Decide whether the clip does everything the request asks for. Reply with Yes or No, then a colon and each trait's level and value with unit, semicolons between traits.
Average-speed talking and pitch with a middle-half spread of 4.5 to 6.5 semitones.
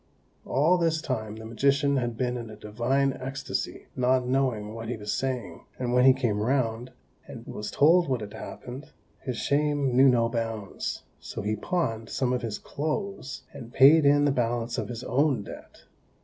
No: average, 180 wpm; average, 3.4 semitones